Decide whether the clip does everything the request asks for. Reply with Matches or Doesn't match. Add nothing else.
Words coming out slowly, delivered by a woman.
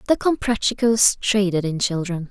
Matches